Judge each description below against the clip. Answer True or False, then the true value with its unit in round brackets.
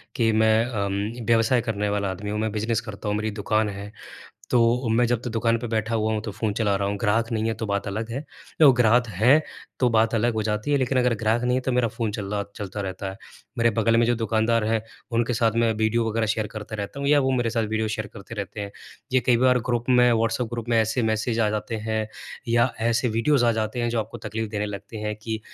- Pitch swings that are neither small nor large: False (1.8 semitones)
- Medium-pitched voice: False (110 Hz)